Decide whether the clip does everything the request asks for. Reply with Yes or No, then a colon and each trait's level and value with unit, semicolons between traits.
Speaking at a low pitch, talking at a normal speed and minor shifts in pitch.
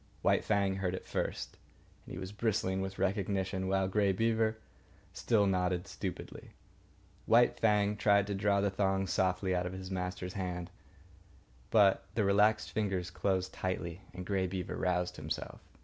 Yes: very low, 95 Hz; average, 155 wpm; narrow, 1.8 semitones